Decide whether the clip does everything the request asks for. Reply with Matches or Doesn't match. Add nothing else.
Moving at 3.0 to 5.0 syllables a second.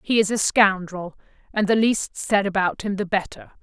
Matches